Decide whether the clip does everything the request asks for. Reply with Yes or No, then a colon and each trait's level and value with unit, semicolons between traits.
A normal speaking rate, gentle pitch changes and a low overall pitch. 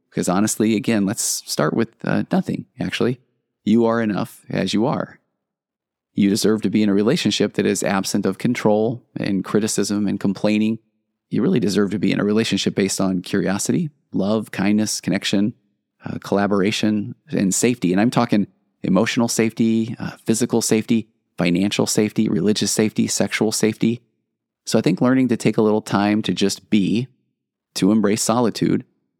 Yes: average, 160 wpm; narrow, 1.9 semitones; low, 110 Hz